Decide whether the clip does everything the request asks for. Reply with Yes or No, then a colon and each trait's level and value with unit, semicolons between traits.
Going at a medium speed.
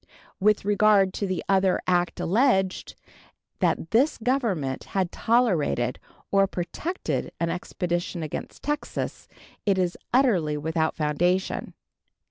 No: slow, 110 wpm